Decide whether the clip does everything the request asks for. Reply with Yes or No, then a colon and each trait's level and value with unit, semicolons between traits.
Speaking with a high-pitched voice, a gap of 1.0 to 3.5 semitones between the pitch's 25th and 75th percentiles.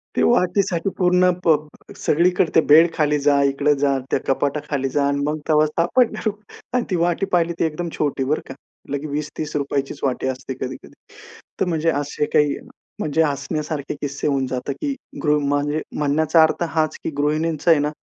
No: medium, 150 Hz; average, 2.7 semitones